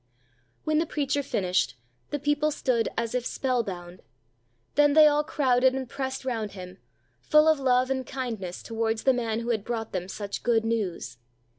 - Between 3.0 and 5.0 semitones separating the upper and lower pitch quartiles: Yes, average, 4.4 semitones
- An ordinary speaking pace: Yes, average, 180 wpm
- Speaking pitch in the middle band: No, high, 240 Hz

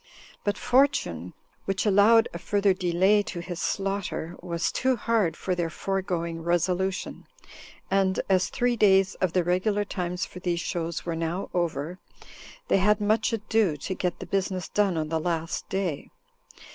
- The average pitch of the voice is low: No, medium, 185 Hz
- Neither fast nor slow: Yes, average, 160 wpm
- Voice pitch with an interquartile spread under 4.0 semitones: Yes, average, 2.9 semitones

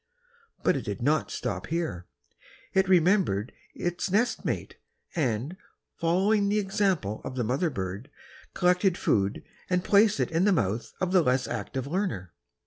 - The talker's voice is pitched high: No, medium, 170 Hz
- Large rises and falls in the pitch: Yes, wide, 8.1 semitones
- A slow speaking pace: No, average, 150 wpm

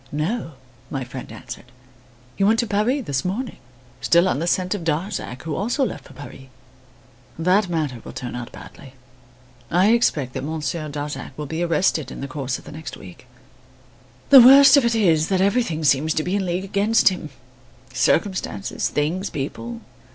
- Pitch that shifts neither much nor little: No, wide, 5.8 semitones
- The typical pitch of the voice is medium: Yes, medium, 170 Hz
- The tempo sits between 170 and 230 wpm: Yes, average, 175 wpm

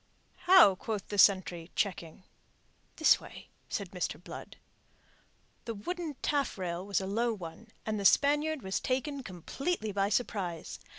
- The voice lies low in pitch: No, high, 205 Hz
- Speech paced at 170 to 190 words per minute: No, slow, 135 wpm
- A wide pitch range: Yes, wide, 6.4 semitones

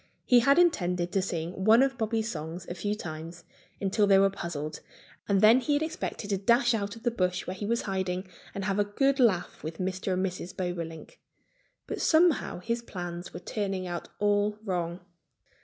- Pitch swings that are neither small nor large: Yes, average, 4.2 semitones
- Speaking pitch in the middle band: No, high, 195 Hz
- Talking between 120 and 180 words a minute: No, average, 190 wpm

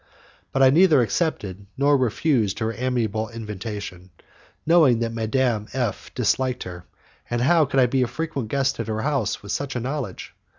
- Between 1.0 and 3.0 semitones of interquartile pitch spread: No, average, 4.0 semitones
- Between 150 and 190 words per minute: Yes, average, 170 wpm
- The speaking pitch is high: No, low, 120 Hz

